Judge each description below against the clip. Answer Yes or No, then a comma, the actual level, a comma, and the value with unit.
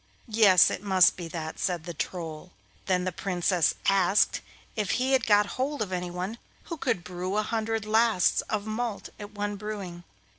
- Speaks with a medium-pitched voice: No, high, 200 Hz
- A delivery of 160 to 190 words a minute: Yes, average, 175 wpm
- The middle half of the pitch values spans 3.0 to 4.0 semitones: Yes, average, 3.3 semitones